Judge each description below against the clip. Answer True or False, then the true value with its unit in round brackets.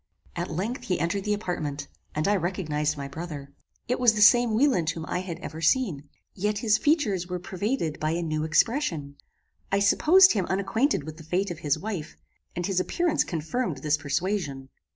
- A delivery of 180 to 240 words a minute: True (185 wpm)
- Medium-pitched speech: True (180 Hz)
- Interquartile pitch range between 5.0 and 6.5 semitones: True (5.5 semitones)